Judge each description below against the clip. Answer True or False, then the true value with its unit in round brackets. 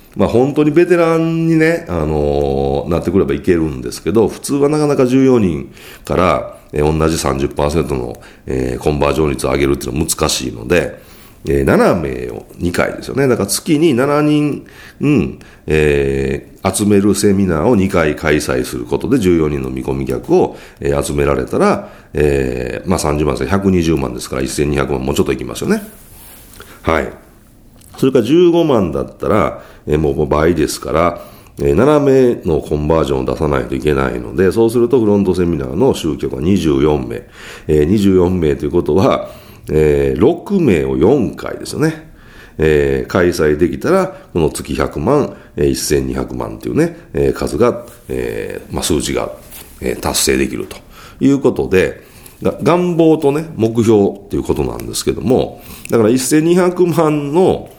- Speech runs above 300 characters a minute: False (290 characters per minute)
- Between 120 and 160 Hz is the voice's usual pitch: False (80 Hz)